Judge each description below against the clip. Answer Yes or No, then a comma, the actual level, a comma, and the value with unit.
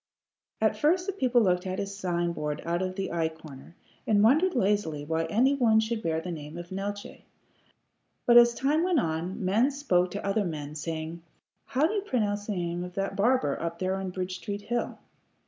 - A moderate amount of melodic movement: No, wide, 5.7 semitones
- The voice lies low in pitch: No, high, 195 Hz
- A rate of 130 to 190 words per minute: No, average, 200 wpm